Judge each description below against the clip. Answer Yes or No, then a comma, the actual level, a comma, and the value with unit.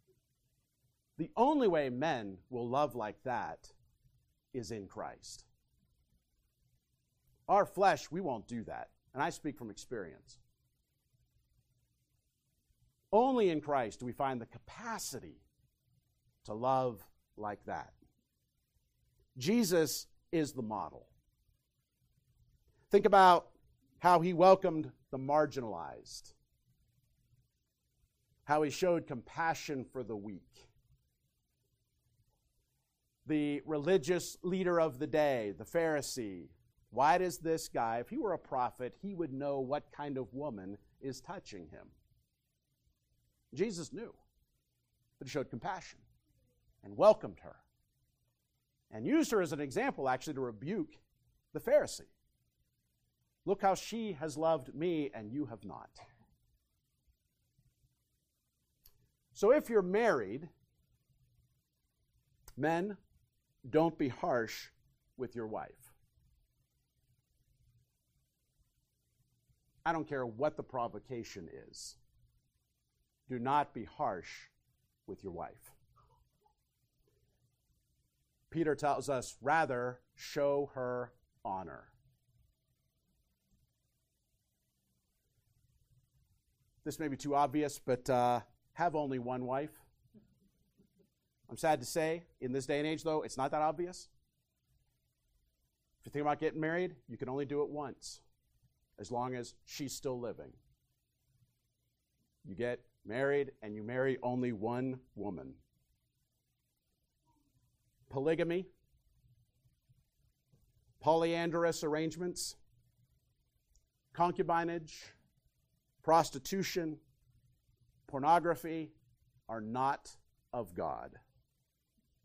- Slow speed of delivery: Yes, slow, 100 wpm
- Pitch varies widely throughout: No, average, 4.6 semitones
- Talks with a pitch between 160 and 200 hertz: No, low, 130 Hz